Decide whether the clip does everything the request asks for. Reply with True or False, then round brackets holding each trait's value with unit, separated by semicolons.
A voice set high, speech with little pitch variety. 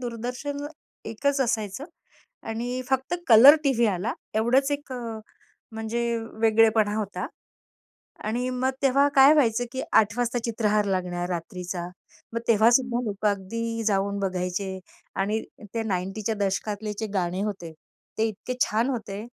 False (220 Hz; 3.5 semitones)